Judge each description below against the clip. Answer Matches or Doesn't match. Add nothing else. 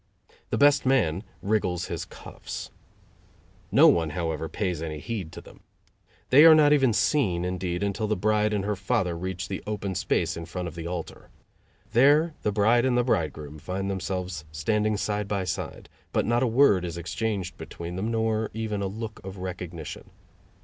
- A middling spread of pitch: Matches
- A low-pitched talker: Matches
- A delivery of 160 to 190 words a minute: Matches